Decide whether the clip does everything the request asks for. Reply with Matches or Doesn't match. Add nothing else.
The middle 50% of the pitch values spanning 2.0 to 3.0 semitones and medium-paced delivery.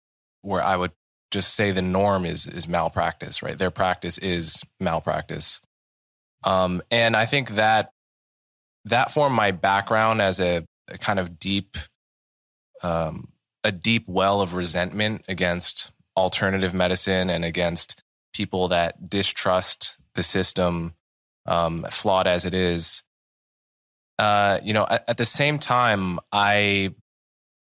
Doesn't match